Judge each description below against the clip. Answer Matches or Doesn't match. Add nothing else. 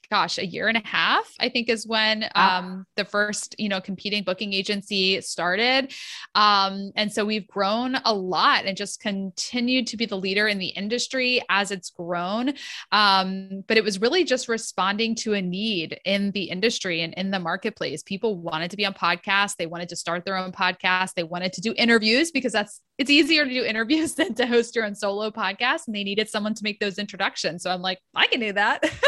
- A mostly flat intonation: Doesn't match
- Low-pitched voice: Doesn't match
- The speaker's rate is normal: Doesn't match